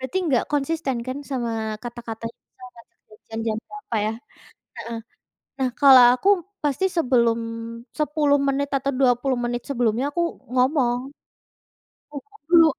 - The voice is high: Yes, very high, 260 Hz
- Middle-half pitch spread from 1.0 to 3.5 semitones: Yes, average, 3.1 semitones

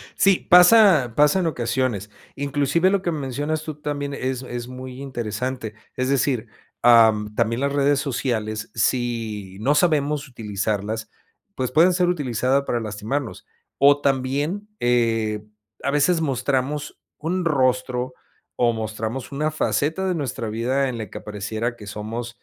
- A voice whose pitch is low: Yes, low, 130 Hz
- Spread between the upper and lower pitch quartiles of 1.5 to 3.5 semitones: No, average, 4.3 semitones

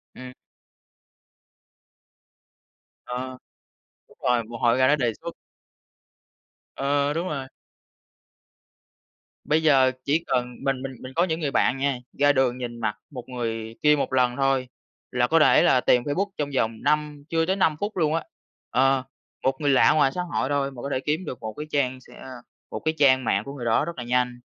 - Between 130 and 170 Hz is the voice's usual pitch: Yes, low, 135 Hz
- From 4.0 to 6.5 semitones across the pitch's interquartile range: No, average, 3.1 semitones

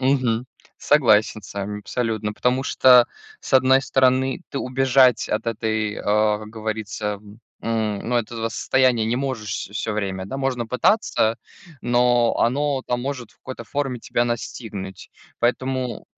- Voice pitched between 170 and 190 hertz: No, low, 120 Hz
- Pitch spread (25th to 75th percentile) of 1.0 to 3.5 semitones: Yes, average, 3.2 semitones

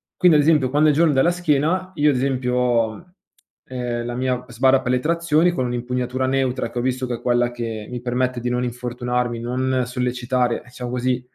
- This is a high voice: No, low, 125 Hz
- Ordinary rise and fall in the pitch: No, narrow, 1.8 semitones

